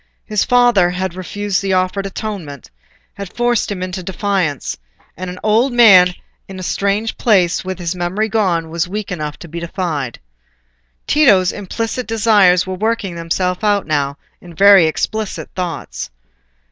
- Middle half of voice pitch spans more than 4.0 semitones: No, average, 3.2 semitones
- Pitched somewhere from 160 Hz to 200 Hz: Yes, medium, 185 Hz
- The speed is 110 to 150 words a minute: Yes, average, 145 wpm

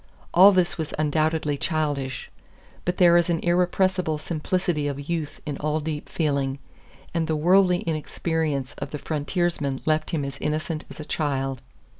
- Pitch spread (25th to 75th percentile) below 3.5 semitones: Yes, average, 2.9 semitones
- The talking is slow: No, average, 155 wpm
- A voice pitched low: No, medium, 155 Hz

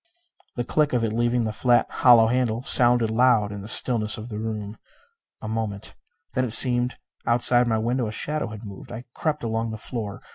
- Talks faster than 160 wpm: Yes, fast, 205 wpm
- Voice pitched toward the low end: Yes, low, 115 Hz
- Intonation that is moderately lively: No, narrow, 2.1 semitones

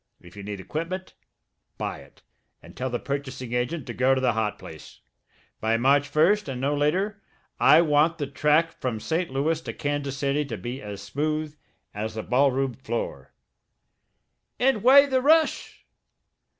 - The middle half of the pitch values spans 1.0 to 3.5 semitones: No, average, 4.8 semitones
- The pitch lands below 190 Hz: Yes, medium, 140 Hz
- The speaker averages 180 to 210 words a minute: No, average, 165 wpm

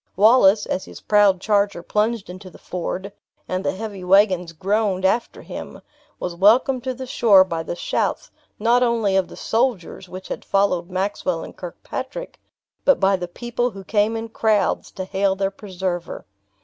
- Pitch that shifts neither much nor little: Yes, average, 3.2 semitones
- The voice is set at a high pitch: Yes, high, 195 Hz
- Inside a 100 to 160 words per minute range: No, average, 170 wpm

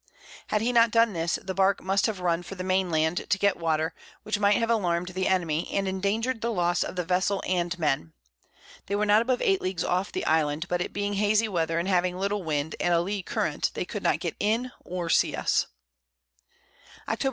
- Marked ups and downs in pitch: No, average, 3.0 semitones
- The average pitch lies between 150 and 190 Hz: Yes, medium, 185 Hz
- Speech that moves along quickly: Yes, fast, 220 wpm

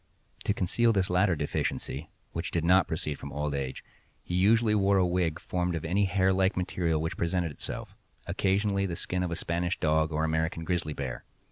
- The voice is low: Yes, very low, 90 Hz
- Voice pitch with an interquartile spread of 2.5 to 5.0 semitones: Yes, average, 2.9 semitones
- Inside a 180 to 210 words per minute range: Yes, average, 190 wpm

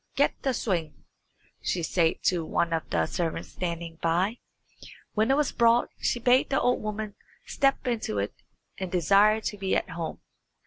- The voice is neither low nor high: No, high, 195 Hz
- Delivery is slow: No, average, 170 wpm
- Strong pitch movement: Yes, wide, 5.7 semitones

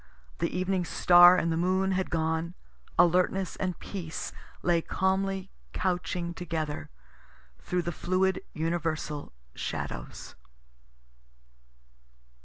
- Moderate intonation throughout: No, narrow, 2.2 semitones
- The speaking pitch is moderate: Yes, medium, 175 Hz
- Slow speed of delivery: Yes, slow, 95 wpm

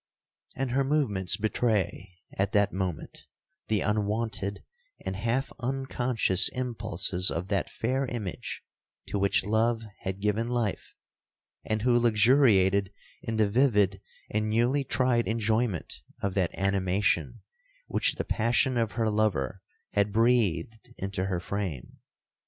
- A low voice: Yes, low, 105 Hz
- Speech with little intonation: No, average, 3.4 semitones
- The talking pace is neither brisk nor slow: No, slow, 125 wpm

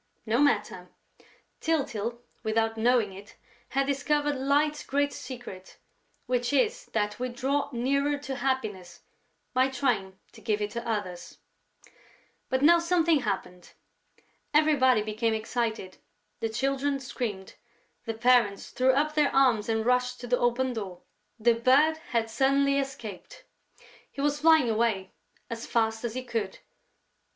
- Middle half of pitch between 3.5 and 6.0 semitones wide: Yes, average, 4.0 semitones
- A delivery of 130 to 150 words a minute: Yes, slow, 135 wpm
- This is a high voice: Yes, high, 245 Hz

